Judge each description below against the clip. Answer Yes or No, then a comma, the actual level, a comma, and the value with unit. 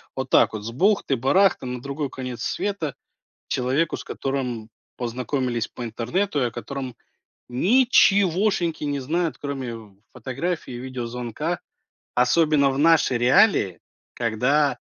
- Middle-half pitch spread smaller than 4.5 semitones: No, average, 5.0 semitones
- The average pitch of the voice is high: No, low, 135 Hz